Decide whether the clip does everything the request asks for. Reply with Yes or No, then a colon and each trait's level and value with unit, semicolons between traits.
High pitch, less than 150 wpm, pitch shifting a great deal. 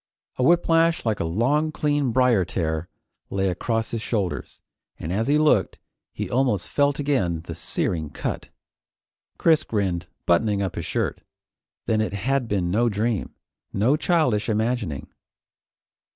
No: low, 110 Hz; average, 140 wpm; wide, 6.7 semitones